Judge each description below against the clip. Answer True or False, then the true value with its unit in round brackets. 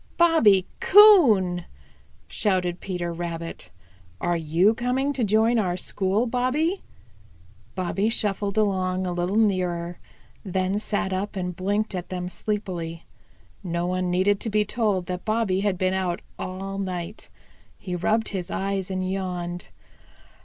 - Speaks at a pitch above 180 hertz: True (190 Hz)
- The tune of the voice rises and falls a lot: False (3.0 semitones)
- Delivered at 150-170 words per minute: False (135 wpm)